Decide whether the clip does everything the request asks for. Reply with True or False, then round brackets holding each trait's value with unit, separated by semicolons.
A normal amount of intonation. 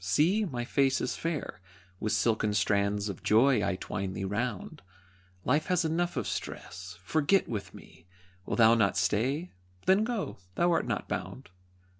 False (8.2 semitones)